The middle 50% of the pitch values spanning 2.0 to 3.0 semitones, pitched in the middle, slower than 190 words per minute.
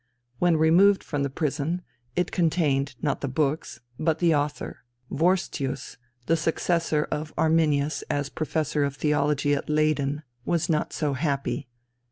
Yes: narrow, 2.4 semitones; medium, 150 Hz; average, 140 wpm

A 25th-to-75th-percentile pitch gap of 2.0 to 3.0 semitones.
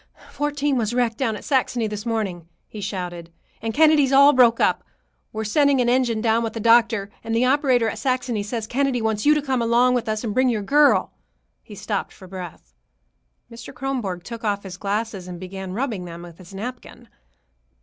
No: average, 3.9 semitones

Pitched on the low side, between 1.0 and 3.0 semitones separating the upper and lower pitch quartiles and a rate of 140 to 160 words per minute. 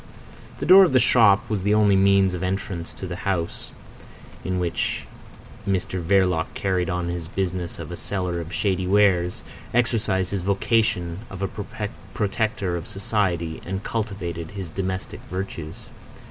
Yes: very low, 95 Hz; narrow, 2.4 semitones; average, 150 wpm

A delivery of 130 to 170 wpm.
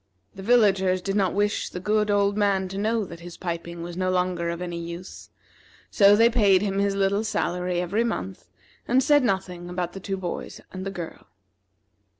No: average, 190 wpm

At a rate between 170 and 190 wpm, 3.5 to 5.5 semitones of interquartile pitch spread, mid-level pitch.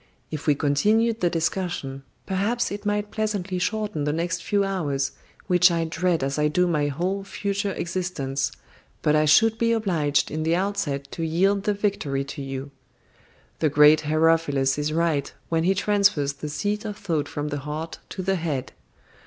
Yes: average, 175 wpm; average, 5.1 semitones; medium, 165 Hz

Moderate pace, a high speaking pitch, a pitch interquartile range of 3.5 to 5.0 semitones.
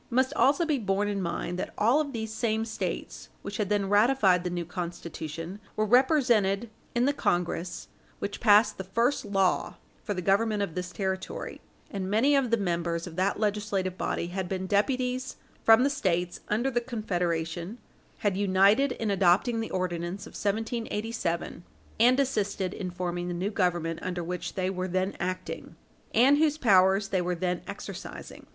Yes: average, 170 wpm; high, 200 Hz; average, 4.0 semitones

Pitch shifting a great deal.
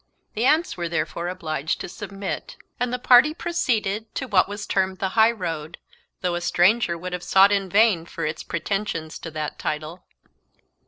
No: average, 4.4 semitones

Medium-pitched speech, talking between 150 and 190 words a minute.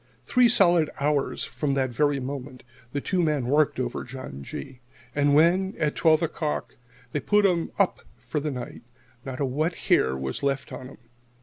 Yes: medium, 145 Hz; average, 185 wpm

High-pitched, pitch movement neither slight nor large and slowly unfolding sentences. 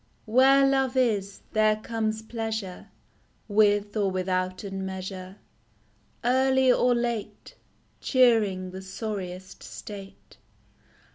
Yes: high, 215 Hz; average, 3.9 semitones; slow, 90 wpm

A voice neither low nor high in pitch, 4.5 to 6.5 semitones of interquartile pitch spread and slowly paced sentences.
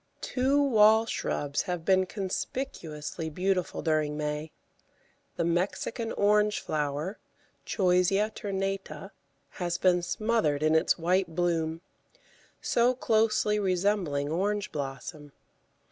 Yes: medium, 180 Hz; average, 4.9 semitones; slow, 100 wpm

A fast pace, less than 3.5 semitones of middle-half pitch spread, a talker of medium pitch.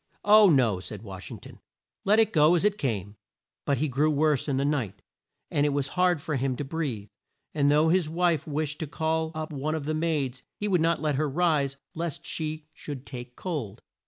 Yes: fast, 215 wpm; average, 3.1 semitones; medium, 150 Hz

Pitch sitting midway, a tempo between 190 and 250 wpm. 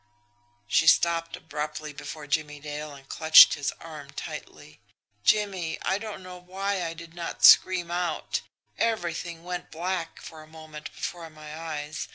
No: medium, 165 Hz; average, 150 wpm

